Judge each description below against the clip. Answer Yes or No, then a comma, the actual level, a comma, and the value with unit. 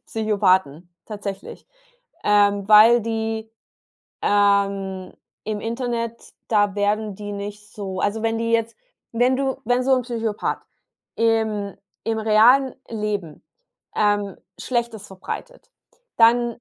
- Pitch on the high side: Yes, high, 215 Hz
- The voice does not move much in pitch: Yes, narrow, 2.1 semitones